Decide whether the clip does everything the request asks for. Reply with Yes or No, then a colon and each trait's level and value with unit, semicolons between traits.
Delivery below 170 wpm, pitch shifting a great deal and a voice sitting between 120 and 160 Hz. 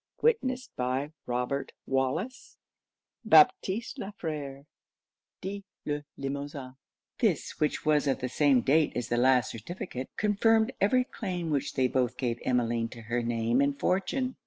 Yes: average, 140 wpm; wide, 7.4 semitones; medium, 140 Hz